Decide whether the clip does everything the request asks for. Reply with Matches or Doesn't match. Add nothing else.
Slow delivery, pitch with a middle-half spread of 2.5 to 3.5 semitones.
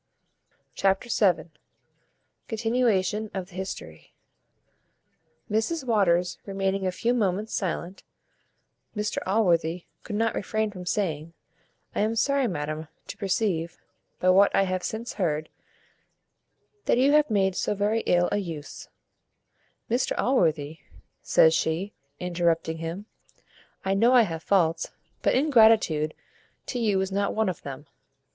Doesn't match